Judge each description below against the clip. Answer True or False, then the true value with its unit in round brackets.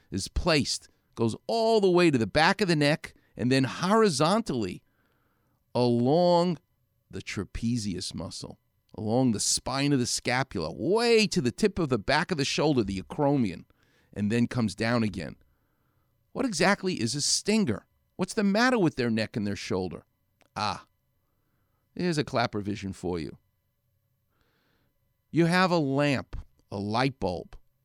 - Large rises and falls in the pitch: True (8.1 semitones)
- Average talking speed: True (150 wpm)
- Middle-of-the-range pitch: False (125 Hz)